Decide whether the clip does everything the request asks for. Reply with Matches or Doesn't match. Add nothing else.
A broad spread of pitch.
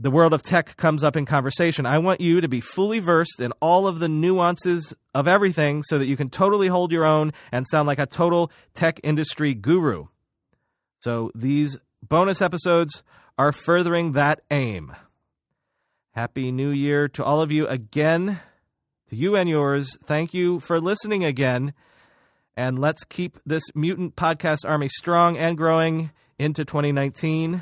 Doesn't match